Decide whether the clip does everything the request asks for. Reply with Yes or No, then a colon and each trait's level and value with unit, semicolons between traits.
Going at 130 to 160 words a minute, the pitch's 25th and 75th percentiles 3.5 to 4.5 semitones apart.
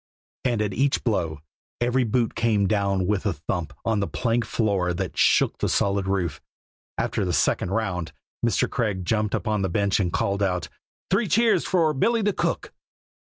No: average, 175 wpm; average, 4.0 semitones